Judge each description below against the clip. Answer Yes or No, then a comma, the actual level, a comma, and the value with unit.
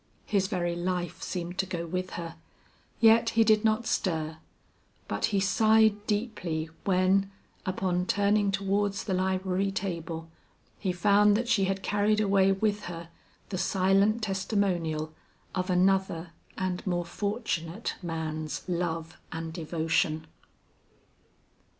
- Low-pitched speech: No, high, 190 Hz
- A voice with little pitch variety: No, average, 3.0 semitones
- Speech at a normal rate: No, slow, 125 wpm